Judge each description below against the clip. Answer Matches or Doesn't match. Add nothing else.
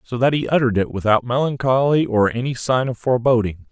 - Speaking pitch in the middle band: Doesn't match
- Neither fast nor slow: Matches